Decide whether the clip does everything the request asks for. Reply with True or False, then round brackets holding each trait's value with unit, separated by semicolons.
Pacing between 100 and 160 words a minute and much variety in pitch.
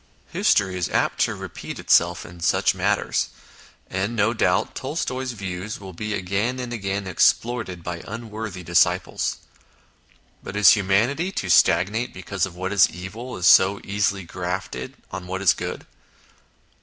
False (145 wpm; 3.3 semitones)